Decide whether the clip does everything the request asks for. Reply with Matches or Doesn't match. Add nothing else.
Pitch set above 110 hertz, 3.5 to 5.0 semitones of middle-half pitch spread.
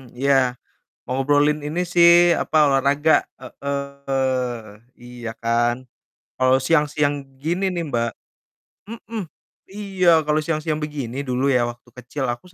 Matches